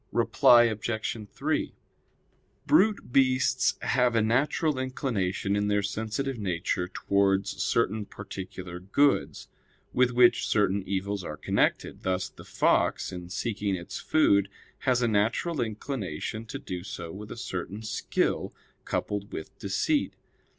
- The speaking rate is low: Yes, slow, 130 wpm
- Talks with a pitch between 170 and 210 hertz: No, low, 105 Hz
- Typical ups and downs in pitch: Yes, average, 4.3 semitones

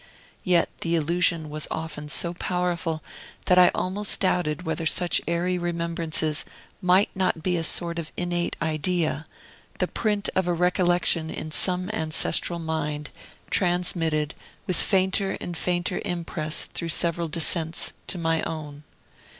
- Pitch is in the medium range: Yes, medium, 170 Hz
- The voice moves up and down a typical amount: No, narrow, 2.1 semitones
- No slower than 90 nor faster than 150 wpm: Yes, slow, 135 wpm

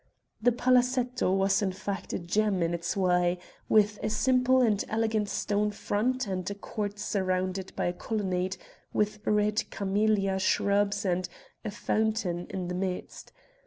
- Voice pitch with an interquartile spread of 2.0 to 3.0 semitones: Yes, narrow, 2.6 semitones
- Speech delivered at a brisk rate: No, average, 150 wpm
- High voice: Yes, high, 205 Hz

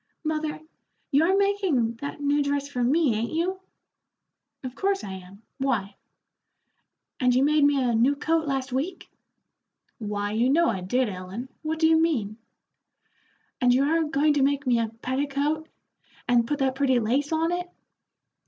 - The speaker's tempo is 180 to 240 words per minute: No, average, 165 wpm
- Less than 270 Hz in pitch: No, very high, 275 Hz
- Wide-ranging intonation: No, average, 4.5 semitones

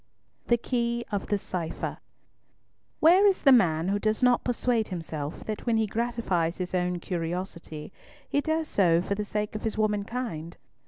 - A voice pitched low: No, high, 210 Hz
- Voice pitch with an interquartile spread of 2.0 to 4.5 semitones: No, average, 5.1 semitones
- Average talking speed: Yes, average, 165 wpm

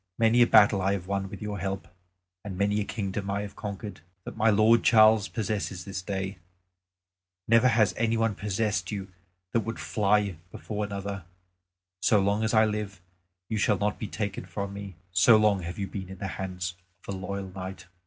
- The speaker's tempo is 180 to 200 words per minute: Yes, average, 195 wpm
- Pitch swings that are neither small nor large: No, narrow, 2.0 semitones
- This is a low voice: Yes, low, 100 Hz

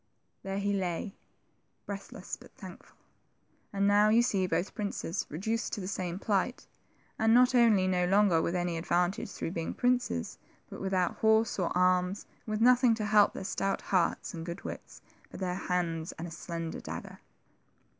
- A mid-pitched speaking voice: No, high, 195 Hz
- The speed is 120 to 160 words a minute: No, average, 170 wpm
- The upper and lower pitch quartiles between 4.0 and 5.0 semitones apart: No, average, 3.1 semitones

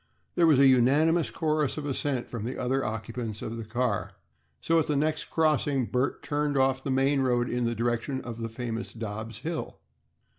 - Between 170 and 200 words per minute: Yes, average, 190 wpm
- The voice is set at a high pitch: No, low, 130 Hz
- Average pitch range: Yes, average, 3.8 semitones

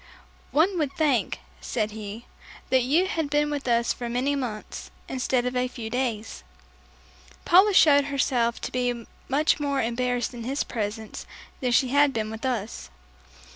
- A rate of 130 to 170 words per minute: Yes, average, 160 wpm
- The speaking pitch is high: Yes, very high, 250 Hz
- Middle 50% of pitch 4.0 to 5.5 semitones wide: No, average, 3.4 semitones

